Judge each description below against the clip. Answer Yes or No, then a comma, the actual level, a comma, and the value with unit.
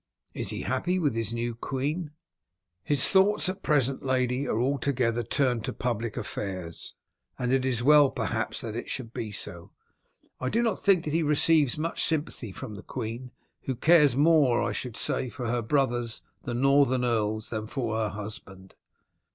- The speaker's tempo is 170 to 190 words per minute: Yes, average, 175 wpm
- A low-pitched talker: Yes, low, 125 Hz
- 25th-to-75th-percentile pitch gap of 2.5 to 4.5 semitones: Yes, average, 4.2 semitones